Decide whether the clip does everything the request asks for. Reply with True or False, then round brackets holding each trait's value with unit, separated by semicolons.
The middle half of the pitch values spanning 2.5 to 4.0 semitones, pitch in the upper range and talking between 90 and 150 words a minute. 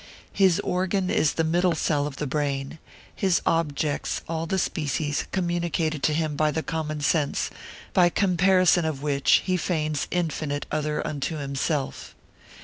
False (2.8 semitones; 155 Hz; 145 wpm)